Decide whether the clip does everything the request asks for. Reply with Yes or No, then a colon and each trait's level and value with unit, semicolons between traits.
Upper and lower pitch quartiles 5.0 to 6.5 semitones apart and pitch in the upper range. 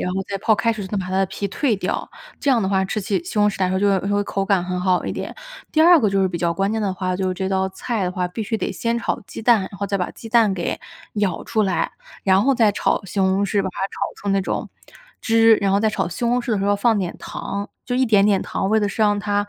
No: narrow, 2.4 semitones; high, 200 Hz